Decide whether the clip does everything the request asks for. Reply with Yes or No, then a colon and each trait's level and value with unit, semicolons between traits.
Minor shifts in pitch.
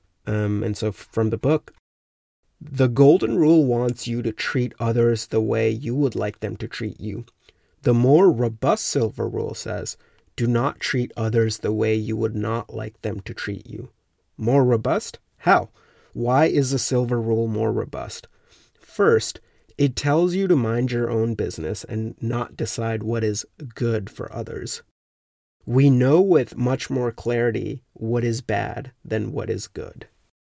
Yes: narrow, 2.3 semitones